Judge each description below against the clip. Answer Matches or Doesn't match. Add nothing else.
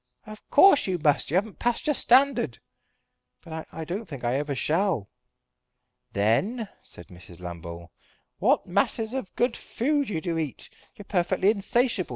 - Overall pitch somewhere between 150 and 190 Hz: Matches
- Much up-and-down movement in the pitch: Matches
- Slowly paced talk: Doesn't match